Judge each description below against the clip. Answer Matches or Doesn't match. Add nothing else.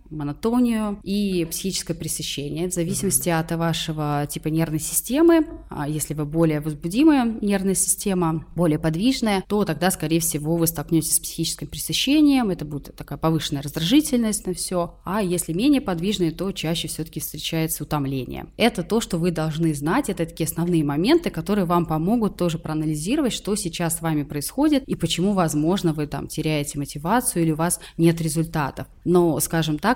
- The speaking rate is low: Doesn't match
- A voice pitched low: Doesn't match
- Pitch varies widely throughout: Doesn't match